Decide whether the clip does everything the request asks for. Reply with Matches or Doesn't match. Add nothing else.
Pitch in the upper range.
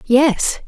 Matches